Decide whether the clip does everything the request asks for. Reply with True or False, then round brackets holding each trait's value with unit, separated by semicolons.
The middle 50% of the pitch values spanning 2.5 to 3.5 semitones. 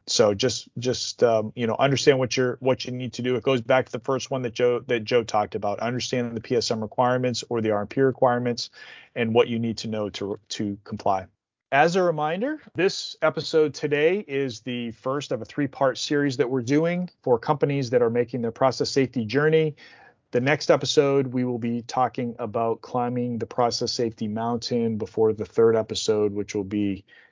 True (2.9 semitones)